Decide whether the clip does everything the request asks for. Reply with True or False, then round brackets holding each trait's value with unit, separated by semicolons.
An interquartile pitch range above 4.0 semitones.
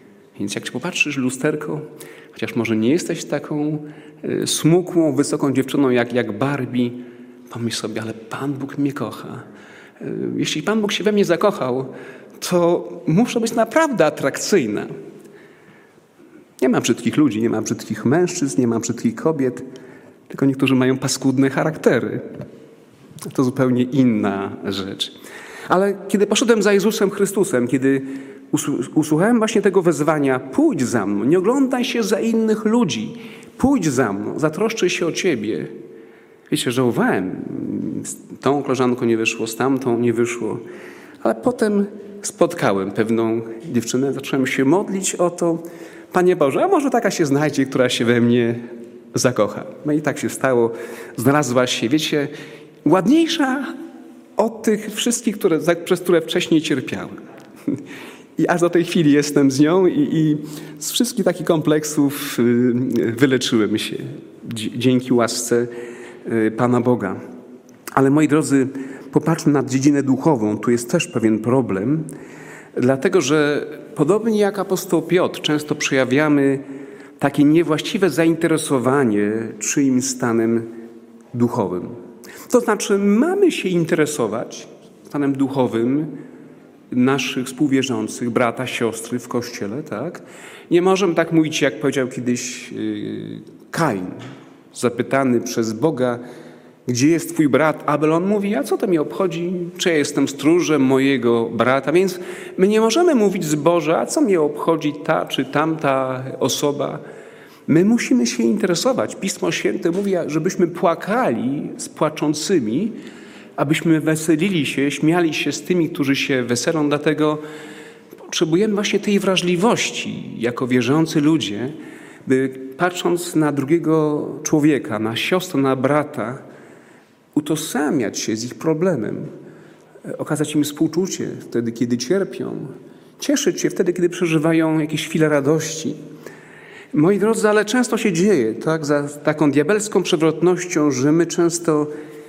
True (5.6 semitones)